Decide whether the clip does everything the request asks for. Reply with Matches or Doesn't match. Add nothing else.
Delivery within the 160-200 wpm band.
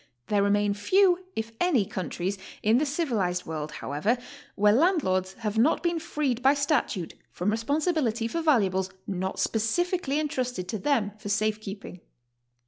Doesn't match